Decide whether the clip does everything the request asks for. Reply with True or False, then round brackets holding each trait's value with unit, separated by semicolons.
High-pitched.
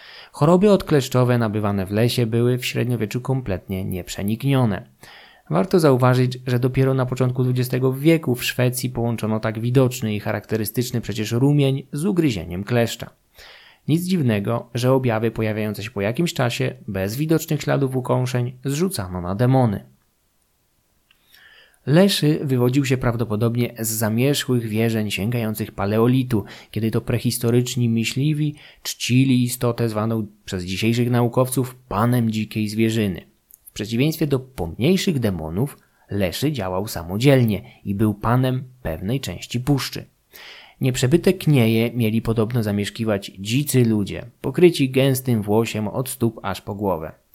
False (120 Hz)